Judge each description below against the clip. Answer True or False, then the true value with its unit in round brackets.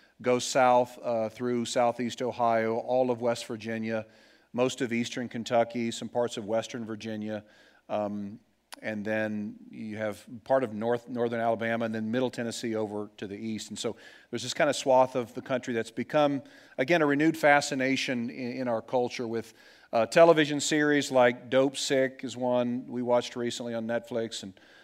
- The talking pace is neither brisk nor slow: True (175 wpm)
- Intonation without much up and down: True (2.2 semitones)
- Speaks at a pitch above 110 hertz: True (120 Hz)